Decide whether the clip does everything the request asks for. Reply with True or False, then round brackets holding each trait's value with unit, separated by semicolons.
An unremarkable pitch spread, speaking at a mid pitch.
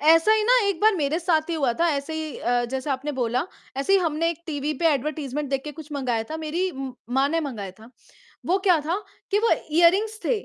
False (3.9 semitones; 310 Hz)